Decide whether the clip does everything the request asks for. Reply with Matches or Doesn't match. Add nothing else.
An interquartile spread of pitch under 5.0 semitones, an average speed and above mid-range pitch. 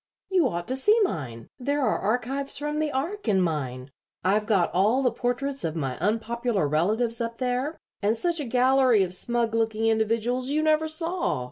Doesn't match